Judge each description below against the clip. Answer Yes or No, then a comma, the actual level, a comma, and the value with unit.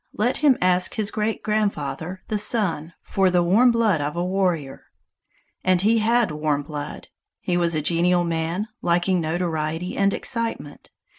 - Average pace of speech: Yes, average, 155 wpm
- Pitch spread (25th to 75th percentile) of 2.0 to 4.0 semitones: No, average, 4.5 semitones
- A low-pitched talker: No, medium, 180 Hz